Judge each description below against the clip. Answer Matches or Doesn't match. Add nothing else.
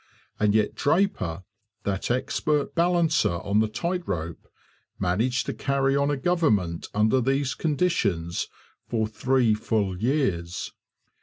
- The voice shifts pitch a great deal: Matches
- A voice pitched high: Doesn't match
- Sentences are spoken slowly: Matches